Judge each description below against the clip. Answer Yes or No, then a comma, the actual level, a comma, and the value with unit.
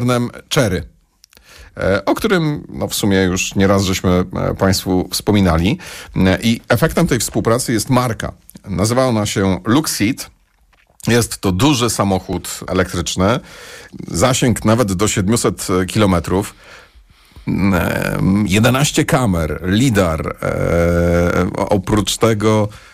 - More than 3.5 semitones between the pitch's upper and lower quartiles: Yes, average, 4.2 semitones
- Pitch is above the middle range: No, low, 100 Hz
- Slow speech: Yes, slow, 90 wpm